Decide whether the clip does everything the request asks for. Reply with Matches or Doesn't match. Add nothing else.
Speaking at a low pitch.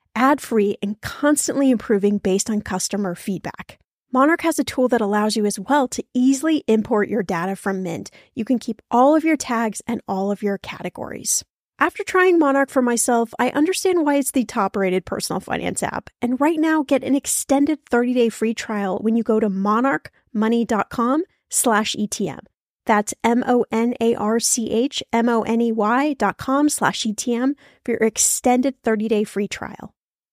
Doesn't match